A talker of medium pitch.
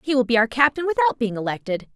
No: very high, 260 Hz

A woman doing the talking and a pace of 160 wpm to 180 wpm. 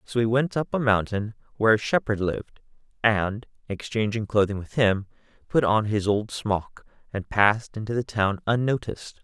No: male; average, 170 wpm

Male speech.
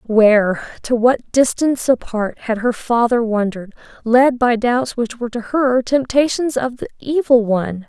No: female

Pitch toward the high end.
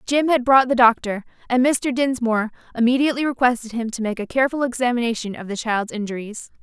Yes: high, 240 Hz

